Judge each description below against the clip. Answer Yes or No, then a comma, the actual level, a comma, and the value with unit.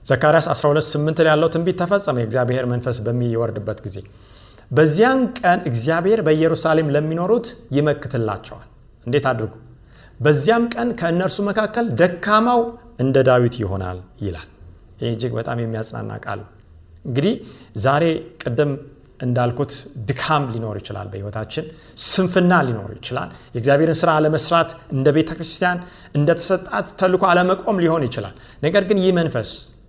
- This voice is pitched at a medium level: Yes, medium, 145 Hz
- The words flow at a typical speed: No, fast, 115 wpm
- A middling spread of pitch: No, wide, 6.4 semitones